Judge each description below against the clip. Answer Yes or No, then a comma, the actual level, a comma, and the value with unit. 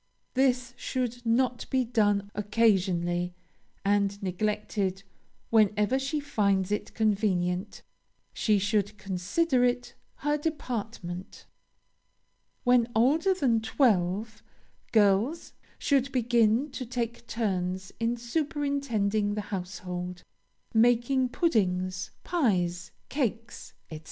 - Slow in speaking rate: Yes, slow, 95 wpm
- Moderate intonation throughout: Yes, average, 4.3 semitones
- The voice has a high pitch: Yes, high, 220 Hz